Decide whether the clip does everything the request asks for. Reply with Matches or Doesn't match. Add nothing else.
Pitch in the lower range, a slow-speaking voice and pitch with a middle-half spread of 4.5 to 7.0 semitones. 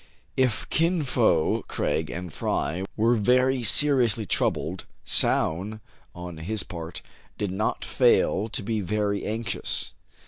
Matches